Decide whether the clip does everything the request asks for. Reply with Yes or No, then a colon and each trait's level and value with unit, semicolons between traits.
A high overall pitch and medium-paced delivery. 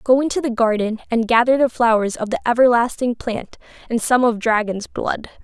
Yes: high, 235 Hz; average, 190 wpm